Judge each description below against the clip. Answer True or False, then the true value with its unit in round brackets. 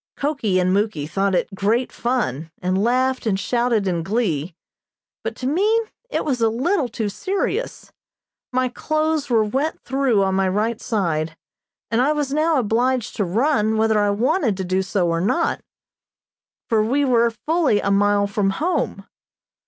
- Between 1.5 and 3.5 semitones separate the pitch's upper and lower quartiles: False (5.1 semitones)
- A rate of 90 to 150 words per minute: False (165 wpm)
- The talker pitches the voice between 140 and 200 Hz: False (225 Hz)